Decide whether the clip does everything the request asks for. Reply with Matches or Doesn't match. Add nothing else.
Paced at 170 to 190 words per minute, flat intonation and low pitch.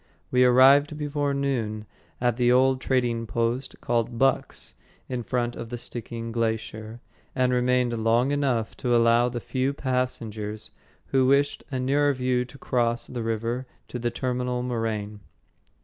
Doesn't match